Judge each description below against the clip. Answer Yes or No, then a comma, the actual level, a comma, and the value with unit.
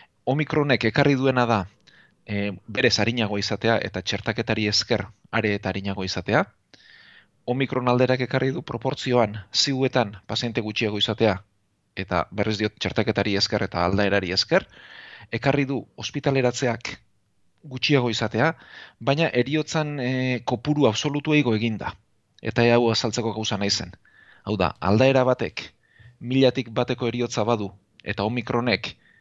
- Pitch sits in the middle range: No, low, 115 Hz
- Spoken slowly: Yes, slow, 120 wpm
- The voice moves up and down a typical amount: Yes, average, 3.8 semitones